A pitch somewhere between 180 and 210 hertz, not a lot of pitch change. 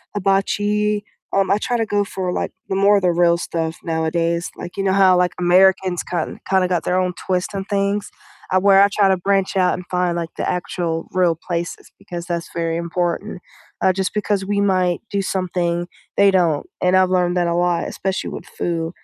Yes: medium, 185 Hz; narrow, 2.1 semitones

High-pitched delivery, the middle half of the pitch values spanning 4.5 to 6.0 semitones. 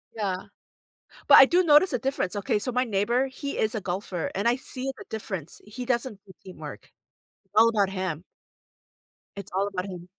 Yes: high, 210 Hz; average, 4.9 semitones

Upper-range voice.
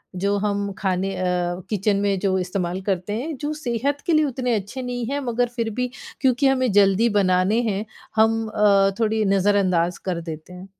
Yes: high, 205 Hz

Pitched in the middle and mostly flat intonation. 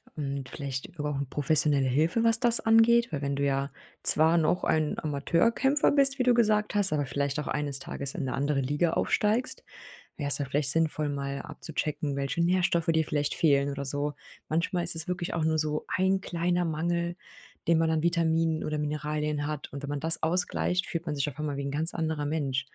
No: medium, 155 Hz; average, 3.3 semitones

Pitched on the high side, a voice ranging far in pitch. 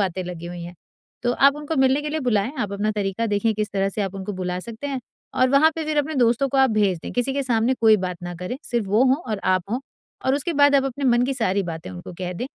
Yes: high, 230 Hz; wide, 5.7 semitones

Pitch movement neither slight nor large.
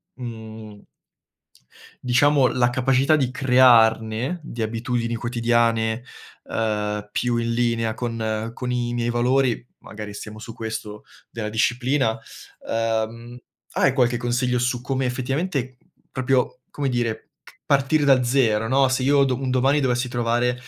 No: narrow, 2.3 semitones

